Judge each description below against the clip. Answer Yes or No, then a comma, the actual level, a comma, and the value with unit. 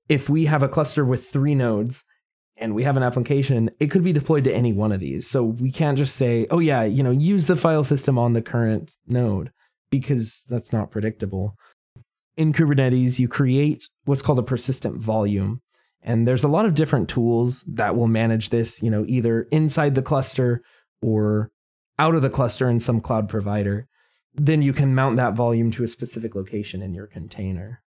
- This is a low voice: Yes, low, 125 Hz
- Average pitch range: Yes, average, 3.9 semitones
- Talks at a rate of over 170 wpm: Yes, average, 195 wpm